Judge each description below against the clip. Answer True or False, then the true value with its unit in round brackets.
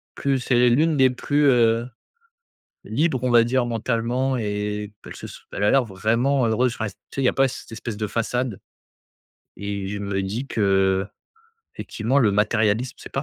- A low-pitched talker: True (115 Hz)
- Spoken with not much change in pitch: False (3.7 semitones)